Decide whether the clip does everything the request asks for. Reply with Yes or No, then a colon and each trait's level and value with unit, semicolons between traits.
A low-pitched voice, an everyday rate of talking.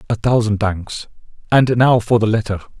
Yes: low, 110 Hz; average, 150 wpm